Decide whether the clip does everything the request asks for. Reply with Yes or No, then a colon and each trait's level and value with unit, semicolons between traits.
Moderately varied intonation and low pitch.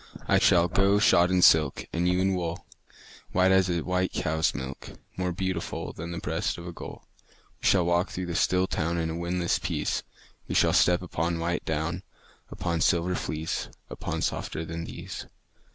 No: narrow, 1.8 semitones; very low, 85 Hz